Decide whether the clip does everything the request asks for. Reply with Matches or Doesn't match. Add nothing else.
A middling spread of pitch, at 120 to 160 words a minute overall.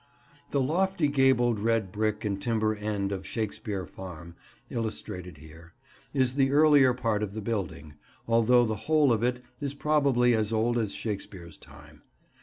Matches